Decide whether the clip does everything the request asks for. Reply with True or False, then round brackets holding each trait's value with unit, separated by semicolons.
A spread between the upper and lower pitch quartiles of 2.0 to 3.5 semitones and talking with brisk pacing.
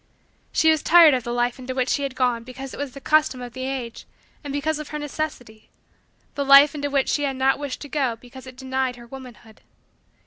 True (2.5 semitones; 230 wpm)